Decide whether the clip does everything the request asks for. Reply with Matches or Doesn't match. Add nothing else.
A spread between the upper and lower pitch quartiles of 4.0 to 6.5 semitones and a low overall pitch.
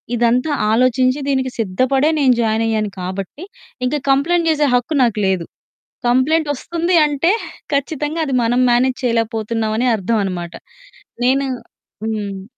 Doesn't match